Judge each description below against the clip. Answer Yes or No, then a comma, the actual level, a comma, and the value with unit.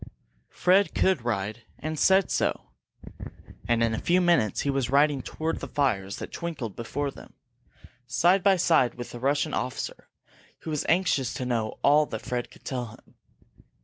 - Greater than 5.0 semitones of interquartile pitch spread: Yes, wide, 5.6 semitones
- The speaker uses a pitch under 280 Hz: Yes, medium, 140 Hz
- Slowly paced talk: No, average, 170 wpm